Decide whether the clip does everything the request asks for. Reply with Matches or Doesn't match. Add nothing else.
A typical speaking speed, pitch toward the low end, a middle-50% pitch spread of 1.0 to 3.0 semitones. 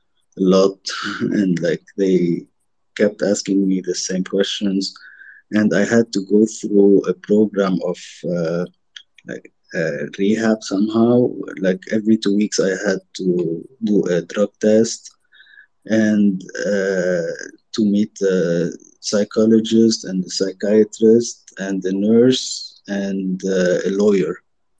Doesn't match